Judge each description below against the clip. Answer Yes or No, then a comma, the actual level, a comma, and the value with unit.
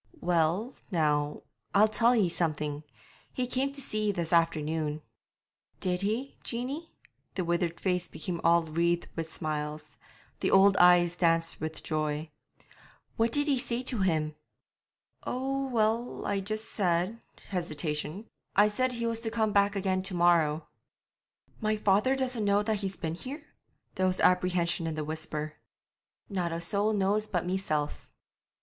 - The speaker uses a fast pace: No, average, 150 wpm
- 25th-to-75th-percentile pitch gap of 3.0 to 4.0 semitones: No, average, 4.8 semitones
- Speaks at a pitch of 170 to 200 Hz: Yes, medium, 185 Hz